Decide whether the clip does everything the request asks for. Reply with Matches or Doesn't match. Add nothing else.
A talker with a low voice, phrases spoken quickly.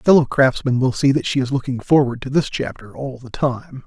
Matches